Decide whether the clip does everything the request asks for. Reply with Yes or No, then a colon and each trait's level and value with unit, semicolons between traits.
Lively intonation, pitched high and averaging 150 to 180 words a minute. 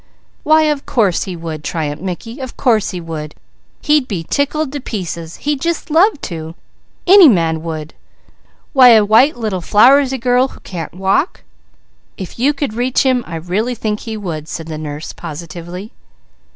Yes: wide, 8.0 semitones; high, 210 Hz; average, 170 wpm